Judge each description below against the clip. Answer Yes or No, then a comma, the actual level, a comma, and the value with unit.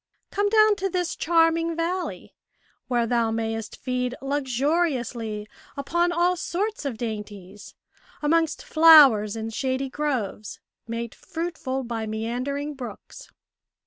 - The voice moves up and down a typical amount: No, wide, 6.5 semitones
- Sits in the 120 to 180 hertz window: No, very high, 270 Hz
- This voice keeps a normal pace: No, slow, 110 wpm